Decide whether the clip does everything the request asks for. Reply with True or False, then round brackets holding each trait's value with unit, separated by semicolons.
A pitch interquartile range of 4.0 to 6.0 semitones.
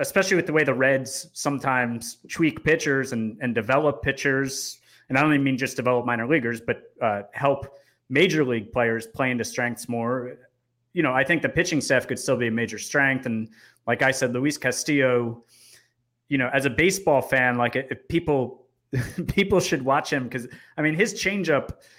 False (3.2 semitones)